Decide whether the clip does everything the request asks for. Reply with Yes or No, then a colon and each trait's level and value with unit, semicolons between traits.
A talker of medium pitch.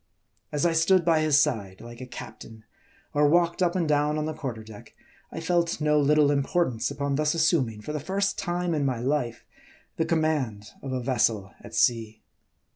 Yes: medium, 150 Hz